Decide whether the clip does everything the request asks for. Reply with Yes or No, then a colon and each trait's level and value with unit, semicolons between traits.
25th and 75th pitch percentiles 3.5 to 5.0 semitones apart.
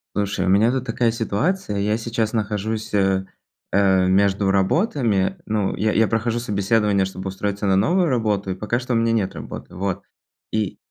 No: average, 2.8 semitones